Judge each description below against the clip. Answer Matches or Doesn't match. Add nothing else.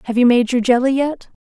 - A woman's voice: Matches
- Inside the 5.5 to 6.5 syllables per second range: Matches